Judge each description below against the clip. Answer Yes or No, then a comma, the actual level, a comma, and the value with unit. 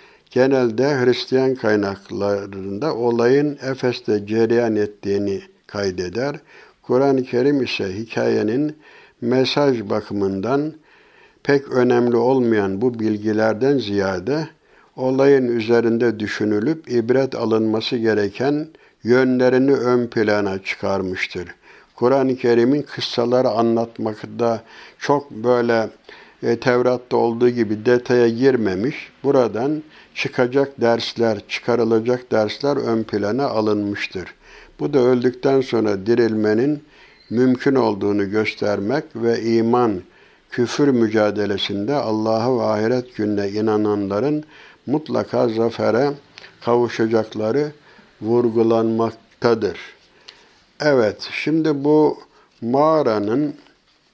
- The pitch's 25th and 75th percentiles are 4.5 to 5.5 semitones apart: No, average, 3.5 semitones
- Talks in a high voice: No, low, 120 Hz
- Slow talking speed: Yes, slow, 85 wpm